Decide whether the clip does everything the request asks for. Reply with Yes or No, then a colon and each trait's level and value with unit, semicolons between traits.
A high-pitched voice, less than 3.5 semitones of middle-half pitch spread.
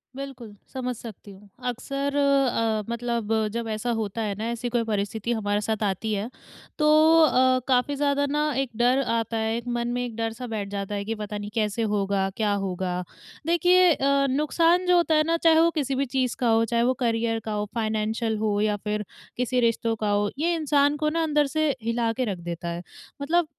No: high, 235 Hz; average, 4.6 semitones